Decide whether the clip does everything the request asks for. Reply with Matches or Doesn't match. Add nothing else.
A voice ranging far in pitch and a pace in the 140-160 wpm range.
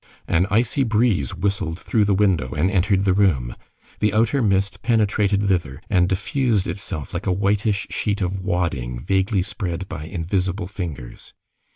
Doesn't match